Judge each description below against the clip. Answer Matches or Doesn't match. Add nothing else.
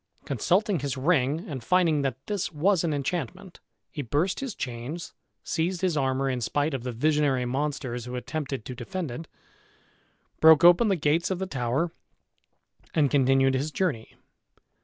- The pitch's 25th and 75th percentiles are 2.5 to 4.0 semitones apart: Doesn't match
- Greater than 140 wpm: Matches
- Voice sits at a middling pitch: Matches